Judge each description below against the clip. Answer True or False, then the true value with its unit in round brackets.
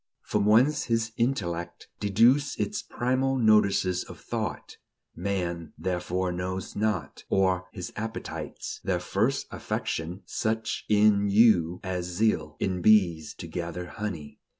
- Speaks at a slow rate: True (125 wpm)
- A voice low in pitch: True (95 Hz)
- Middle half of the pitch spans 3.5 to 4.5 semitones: True (3.9 semitones)